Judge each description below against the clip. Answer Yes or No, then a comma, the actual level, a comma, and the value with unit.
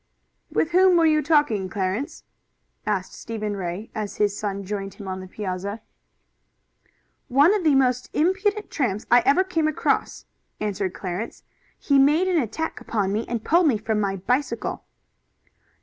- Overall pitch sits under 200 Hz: No, high, 230 Hz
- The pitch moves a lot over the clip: Yes, wide, 7.4 semitones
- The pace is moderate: Yes, average, 155 wpm